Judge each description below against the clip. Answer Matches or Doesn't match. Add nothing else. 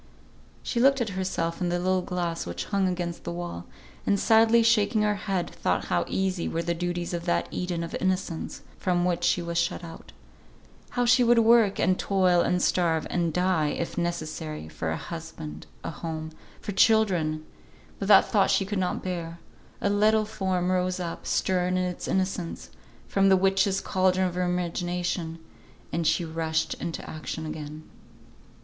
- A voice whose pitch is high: Doesn't match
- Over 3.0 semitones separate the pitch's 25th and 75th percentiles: Doesn't match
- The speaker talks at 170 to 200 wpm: Matches